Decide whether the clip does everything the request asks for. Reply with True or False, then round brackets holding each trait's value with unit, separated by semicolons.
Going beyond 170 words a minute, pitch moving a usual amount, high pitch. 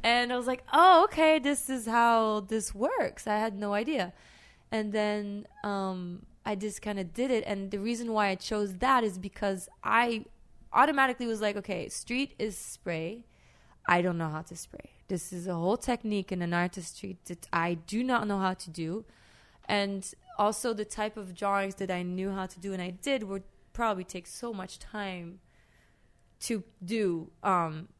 True (190 wpm; 3.5 semitones; 205 Hz)